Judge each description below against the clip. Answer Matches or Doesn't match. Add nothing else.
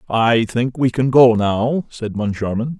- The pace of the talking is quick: Doesn't match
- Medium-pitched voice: Doesn't match